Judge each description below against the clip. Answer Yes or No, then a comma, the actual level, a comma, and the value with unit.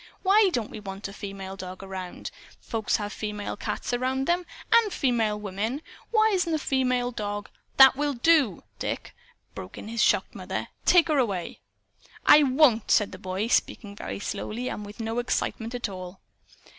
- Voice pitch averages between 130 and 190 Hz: No, high, 230 Hz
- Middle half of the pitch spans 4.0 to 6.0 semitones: Yes, average, 5.0 semitones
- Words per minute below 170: No, average, 175 wpm